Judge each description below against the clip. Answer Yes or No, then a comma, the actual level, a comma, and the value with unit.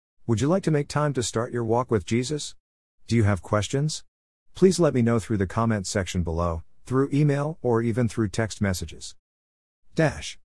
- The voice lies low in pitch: Yes, low, 115 Hz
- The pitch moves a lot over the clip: Yes, wide, 7.0 semitones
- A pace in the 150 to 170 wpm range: No, average, 190 wpm